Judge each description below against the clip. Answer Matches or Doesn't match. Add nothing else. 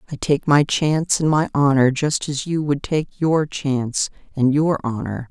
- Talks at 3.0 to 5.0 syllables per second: Matches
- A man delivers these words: Doesn't match